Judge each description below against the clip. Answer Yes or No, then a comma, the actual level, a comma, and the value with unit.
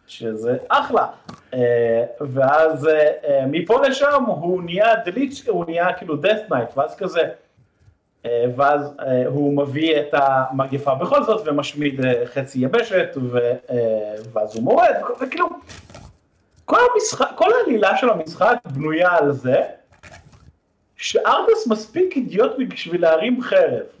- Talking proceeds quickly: No, average, 125 wpm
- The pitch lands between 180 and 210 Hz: No, medium, 160 Hz